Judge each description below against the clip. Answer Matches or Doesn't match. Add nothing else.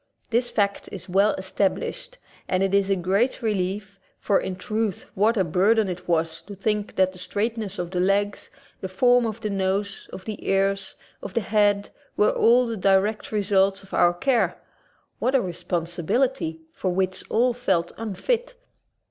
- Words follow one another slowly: Doesn't match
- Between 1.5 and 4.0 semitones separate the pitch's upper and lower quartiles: Matches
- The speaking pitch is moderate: Doesn't match